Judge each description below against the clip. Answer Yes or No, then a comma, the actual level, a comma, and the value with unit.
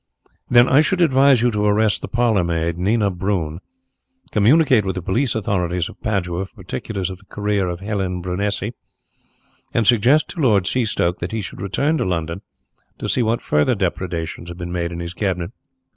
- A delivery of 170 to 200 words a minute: Yes, average, 180 wpm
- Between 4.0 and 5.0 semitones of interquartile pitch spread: Yes, average, 4.6 semitones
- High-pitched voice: No, low, 100 Hz